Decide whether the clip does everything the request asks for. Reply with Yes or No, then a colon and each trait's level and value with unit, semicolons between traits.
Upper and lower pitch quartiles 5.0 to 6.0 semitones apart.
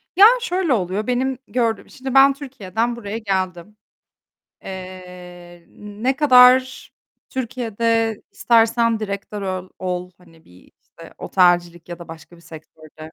Yes: wide, 5.6 semitones